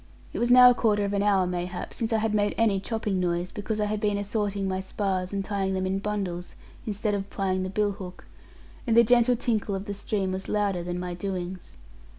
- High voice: Yes, high, 200 Hz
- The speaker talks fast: Yes, fast, 225 wpm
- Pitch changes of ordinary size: No, narrow, 2.1 semitones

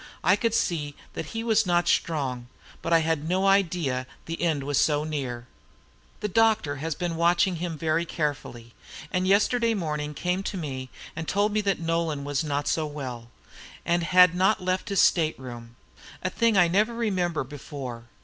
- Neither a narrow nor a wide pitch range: Yes, average, 4.3 semitones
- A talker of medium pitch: Yes, medium, 165 Hz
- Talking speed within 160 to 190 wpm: Yes, average, 180 wpm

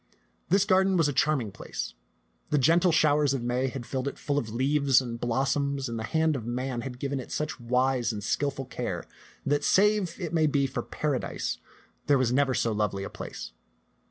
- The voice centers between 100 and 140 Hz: Yes, low, 135 Hz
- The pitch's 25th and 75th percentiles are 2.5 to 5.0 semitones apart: Yes, average, 3.5 semitones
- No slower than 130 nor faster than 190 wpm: No, average, 200 wpm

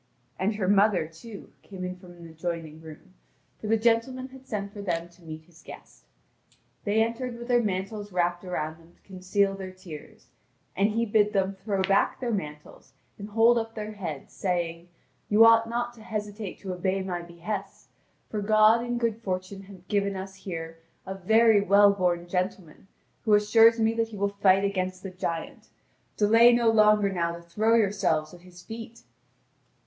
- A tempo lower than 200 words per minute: Yes, average, 180 wpm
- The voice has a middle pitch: No, high, 200 Hz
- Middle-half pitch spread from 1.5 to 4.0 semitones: Yes, average, 3.5 semitones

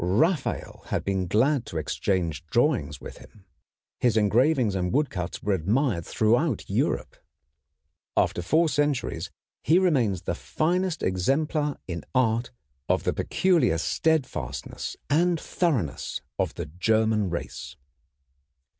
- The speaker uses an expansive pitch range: Yes, wide, 8.7 semitones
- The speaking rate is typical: No, slow, 120 wpm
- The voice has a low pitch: Yes, low, 115 Hz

